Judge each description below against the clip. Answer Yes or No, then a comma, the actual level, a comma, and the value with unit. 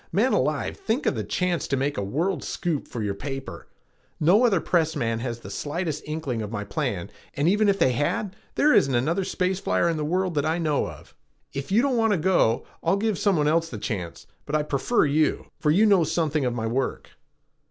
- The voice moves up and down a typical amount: No, wide, 5.7 semitones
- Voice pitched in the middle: Yes, medium, 155 Hz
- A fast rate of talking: Yes, fast, 225 wpm